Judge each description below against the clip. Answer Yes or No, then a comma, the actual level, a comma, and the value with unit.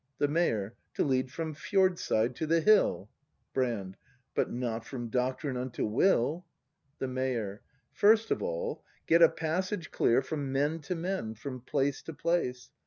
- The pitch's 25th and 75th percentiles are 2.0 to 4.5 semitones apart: No, average, 5.2 semitones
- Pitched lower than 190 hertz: Yes, medium, 140 Hz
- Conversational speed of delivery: Yes, average, 155 wpm